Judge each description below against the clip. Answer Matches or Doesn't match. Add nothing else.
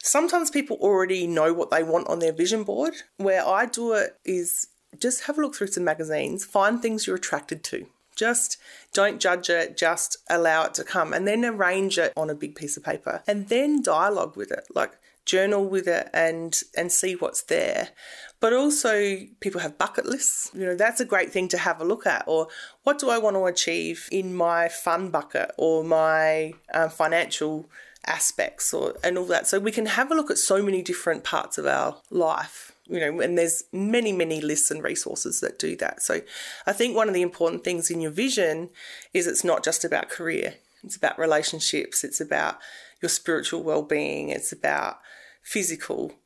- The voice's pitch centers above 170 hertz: Matches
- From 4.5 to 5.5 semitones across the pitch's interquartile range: Matches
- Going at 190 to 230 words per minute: Matches